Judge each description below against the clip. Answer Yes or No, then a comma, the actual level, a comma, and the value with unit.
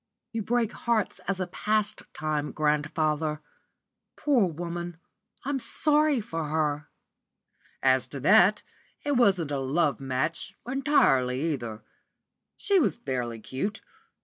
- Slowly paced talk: Yes, slow, 115 wpm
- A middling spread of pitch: No, wide, 7.0 semitones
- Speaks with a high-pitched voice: No, medium, 165 Hz